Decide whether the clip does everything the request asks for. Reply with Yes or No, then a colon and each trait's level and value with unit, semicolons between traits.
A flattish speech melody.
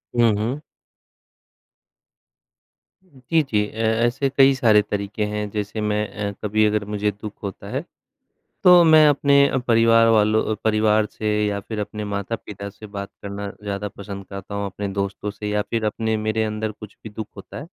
Yes: narrow, 1.9 semitones